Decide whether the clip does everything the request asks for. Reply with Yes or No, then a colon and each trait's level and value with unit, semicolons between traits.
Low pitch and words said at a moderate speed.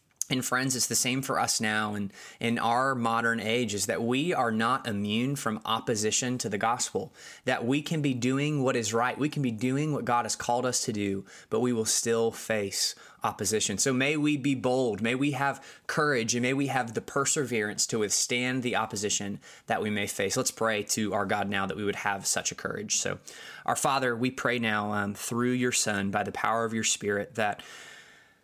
No: low, 120 Hz; fast, 215 wpm